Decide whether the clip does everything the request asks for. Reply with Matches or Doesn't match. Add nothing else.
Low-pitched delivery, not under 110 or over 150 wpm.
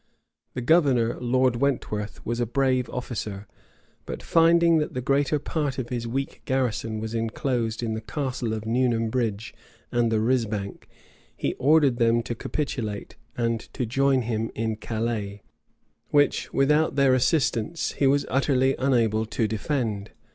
Matches